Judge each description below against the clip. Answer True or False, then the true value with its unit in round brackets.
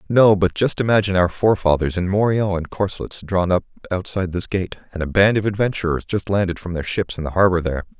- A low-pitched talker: True (95 Hz)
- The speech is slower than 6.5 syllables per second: False (6.9 syllables/s)